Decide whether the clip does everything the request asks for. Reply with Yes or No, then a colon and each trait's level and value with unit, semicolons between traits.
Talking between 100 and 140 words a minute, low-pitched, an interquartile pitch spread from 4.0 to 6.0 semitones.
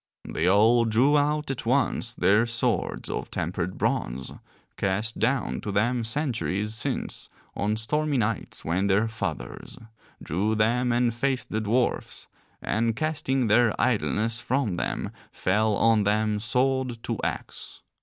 No: slow, 135 wpm; low, 115 Hz; average, 3.1 semitones